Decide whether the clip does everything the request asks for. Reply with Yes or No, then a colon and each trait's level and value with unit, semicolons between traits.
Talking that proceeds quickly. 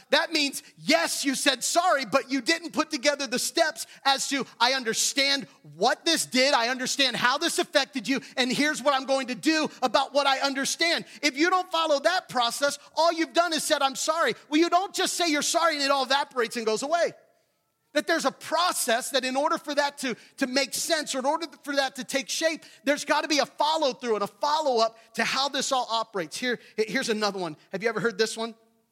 Yes: fast, 225 wpm